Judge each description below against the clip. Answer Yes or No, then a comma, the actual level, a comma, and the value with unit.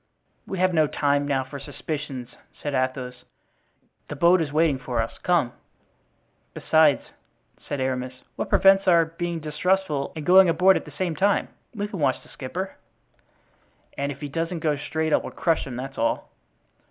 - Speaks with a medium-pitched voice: Yes, medium, 150 Hz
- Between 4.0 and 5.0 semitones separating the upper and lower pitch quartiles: Yes, average, 4.3 semitones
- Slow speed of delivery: No, average, 170 wpm